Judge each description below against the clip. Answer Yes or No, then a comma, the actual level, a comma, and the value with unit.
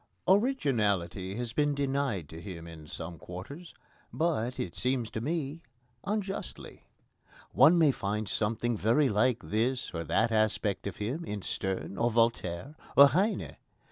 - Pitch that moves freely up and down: Yes, wide, 6.3 semitones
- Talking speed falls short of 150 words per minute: Yes, average, 140 wpm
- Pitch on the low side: Yes, low, 115 Hz